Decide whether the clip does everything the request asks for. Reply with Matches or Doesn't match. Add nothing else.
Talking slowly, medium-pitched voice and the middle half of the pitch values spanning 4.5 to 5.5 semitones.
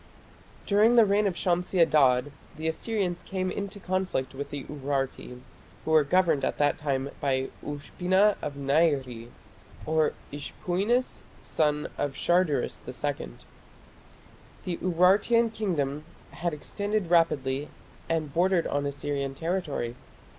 Matches